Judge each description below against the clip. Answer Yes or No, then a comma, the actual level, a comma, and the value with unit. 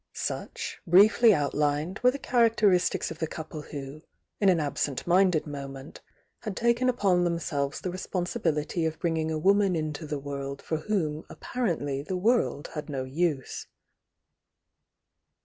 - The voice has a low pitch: No, medium, 165 Hz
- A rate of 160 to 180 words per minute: No, average, 145 wpm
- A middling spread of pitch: Yes, average, 4.7 semitones